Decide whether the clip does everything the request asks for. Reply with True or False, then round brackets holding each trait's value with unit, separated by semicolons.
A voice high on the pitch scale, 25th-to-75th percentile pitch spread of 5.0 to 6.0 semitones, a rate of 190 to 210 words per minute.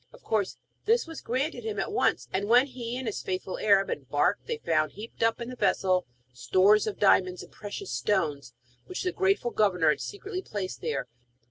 True (215 Hz; 5.6 semitones; 195 wpm)